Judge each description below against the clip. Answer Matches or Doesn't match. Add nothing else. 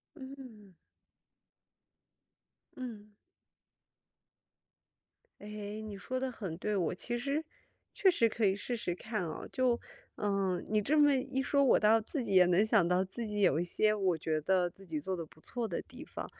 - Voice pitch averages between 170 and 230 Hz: Matches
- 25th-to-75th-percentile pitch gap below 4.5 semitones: Doesn't match